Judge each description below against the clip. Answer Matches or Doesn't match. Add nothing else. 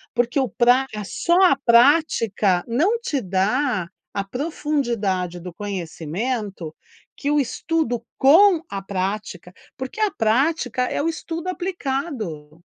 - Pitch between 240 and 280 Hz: Matches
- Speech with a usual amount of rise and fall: Doesn't match